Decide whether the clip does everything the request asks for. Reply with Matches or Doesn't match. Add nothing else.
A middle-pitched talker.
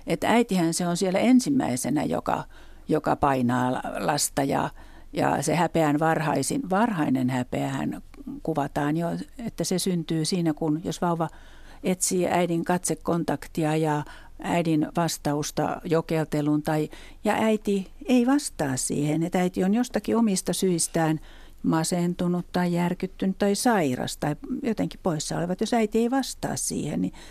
Matches